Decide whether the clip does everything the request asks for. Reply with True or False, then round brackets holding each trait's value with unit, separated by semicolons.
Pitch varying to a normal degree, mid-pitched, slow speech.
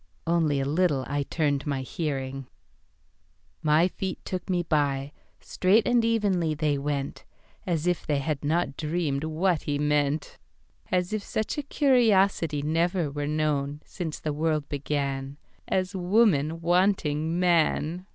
True (3.8 semitones; 155 Hz; 120 wpm)